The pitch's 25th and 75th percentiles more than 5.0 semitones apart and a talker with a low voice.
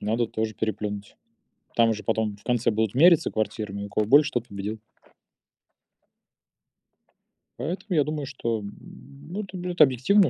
Yes: wide, 5.6 semitones; low, 115 Hz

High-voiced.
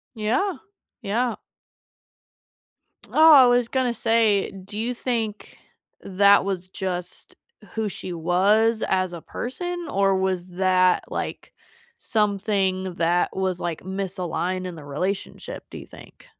Yes: high, 195 Hz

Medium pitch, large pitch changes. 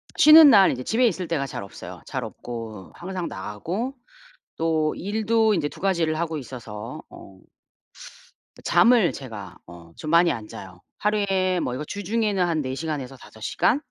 Yes: medium, 165 Hz; wide, 8.4 semitones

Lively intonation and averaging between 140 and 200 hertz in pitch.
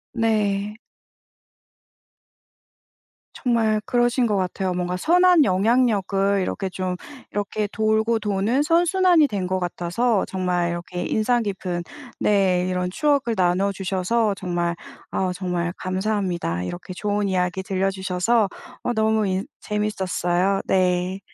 No: average, 3.2 semitones; high, 195 Hz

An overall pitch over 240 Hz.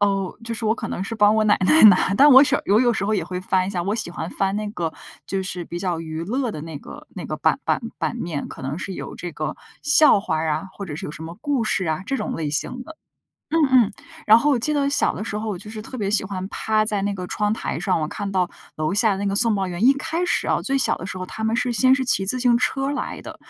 No: high, 205 Hz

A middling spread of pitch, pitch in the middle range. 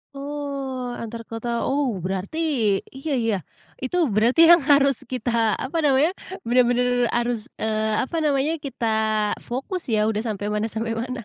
No: average, 3.7 semitones; high, 245 Hz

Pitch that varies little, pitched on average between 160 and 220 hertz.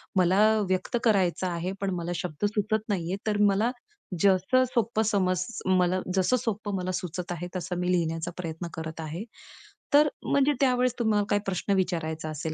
No: average, 3.3 semitones; medium, 185 Hz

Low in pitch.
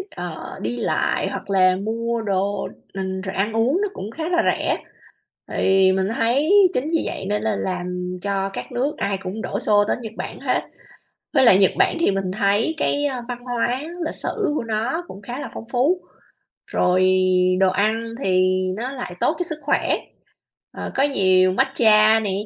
No: high, 215 Hz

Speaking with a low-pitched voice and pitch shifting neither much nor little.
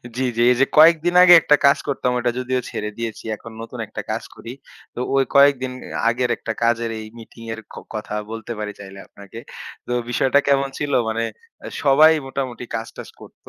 Yes: low, 125 Hz; average, 3.4 semitones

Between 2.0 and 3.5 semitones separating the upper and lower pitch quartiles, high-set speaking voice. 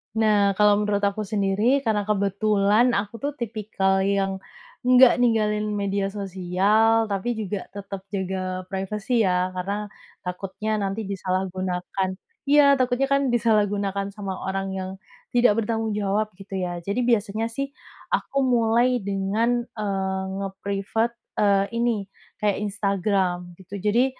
Yes: narrow, 2.6 semitones; high, 205 Hz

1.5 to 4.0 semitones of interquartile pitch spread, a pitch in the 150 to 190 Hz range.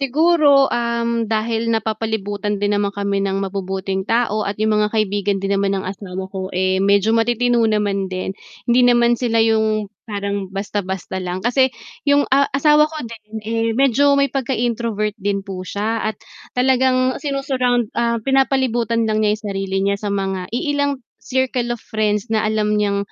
No: average, 3.4 semitones; high, 220 Hz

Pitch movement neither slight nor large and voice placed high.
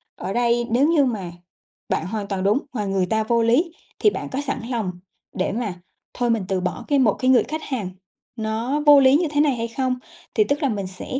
Yes: average, 5.0 semitones; high, 235 Hz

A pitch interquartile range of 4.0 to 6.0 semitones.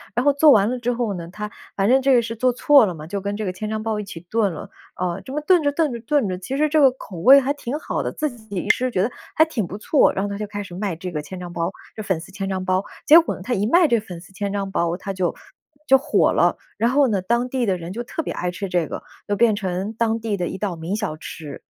Yes: average, 5.2 semitones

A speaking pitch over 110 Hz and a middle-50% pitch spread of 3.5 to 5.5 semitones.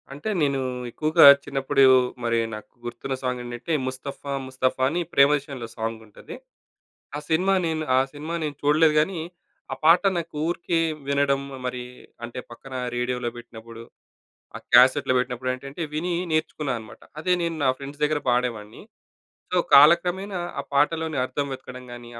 Yes: medium, 140 Hz; average, 4.0 semitones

